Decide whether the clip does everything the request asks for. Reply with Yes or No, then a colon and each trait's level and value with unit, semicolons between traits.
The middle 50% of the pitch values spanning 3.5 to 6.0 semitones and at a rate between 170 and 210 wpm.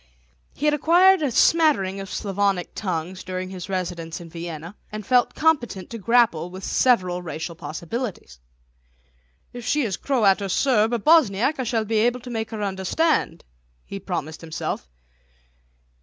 No: wide, 5.5 semitones; average, 155 wpm